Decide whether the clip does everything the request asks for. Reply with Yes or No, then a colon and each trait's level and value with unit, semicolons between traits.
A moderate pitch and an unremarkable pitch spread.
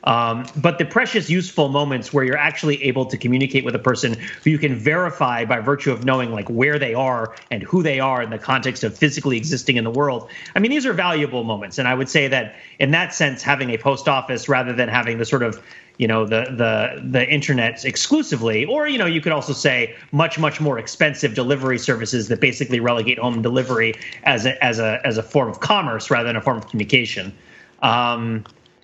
No: low, 130 Hz; average, 3.9 semitones